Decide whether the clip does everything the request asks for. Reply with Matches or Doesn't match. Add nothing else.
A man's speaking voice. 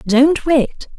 Doesn't match